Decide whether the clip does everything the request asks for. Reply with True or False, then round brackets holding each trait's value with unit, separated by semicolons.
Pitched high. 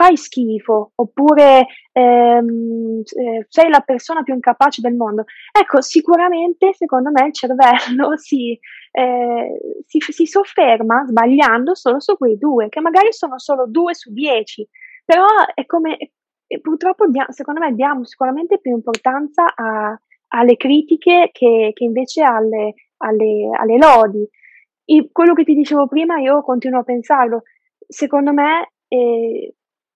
True (270 Hz)